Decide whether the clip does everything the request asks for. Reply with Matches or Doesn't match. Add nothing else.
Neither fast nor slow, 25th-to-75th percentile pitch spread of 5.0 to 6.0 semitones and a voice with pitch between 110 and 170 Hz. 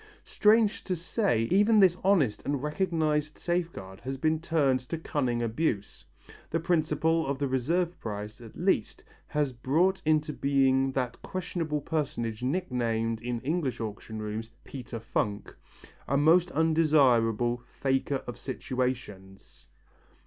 Doesn't match